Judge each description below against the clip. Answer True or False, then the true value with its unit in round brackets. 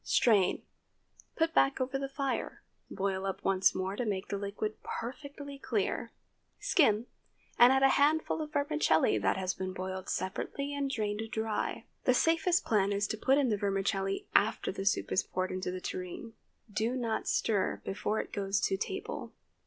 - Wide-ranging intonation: True (6.0 semitones)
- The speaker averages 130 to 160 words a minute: False (170 wpm)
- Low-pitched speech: False (215 Hz)